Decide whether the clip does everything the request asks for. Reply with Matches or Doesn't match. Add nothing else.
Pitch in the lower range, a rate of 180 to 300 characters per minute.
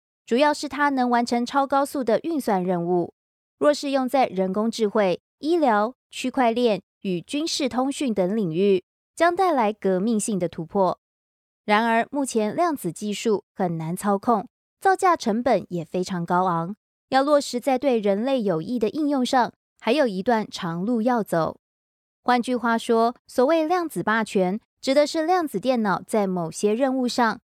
Doesn't match